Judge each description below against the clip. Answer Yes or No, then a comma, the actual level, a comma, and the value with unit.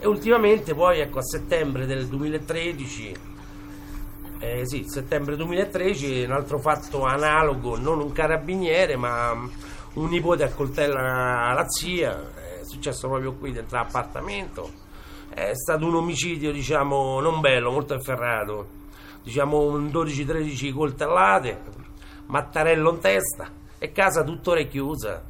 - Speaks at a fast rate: No, average, 125 wpm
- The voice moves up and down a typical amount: Yes, average, 4.1 semitones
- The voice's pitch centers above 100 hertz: Yes, medium, 140 Hz